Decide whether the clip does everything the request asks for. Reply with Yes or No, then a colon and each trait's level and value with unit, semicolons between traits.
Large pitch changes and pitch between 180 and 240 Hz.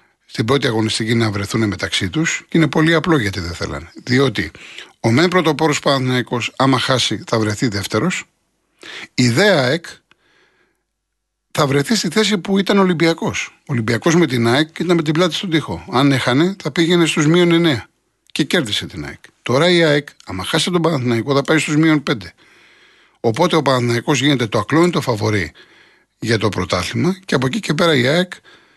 No: wide, 6.2 semitones; medium, 140 Hz